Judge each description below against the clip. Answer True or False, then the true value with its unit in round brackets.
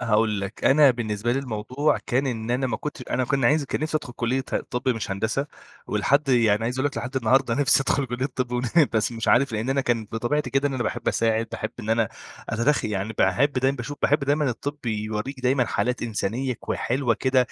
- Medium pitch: False (125 Hz)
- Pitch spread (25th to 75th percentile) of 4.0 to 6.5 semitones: False (3.2 semitones)